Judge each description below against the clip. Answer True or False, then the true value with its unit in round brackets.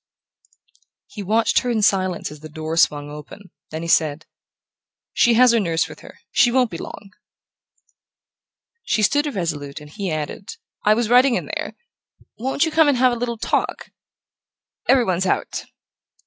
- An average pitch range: False (7.0 semitones)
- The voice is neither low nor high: False (205 Hz)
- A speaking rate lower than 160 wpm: False (165 wpm)